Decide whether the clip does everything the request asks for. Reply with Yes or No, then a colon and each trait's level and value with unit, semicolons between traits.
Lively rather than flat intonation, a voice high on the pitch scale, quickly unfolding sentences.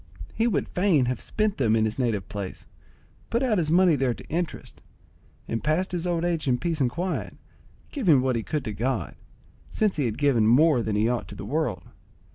No: wide, 7.0 semitones; medium, 140 Hz; fast, 210 wpm